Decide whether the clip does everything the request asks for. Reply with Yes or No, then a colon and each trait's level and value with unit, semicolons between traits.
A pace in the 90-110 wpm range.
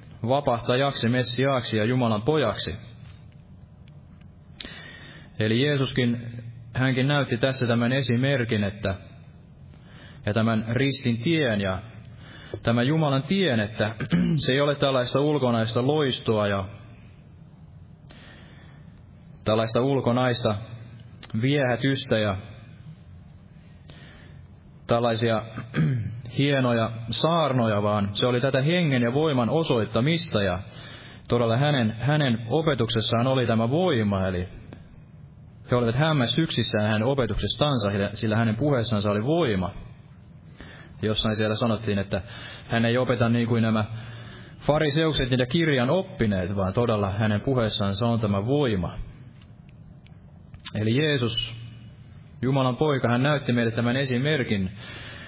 Yes: average, 100 wpm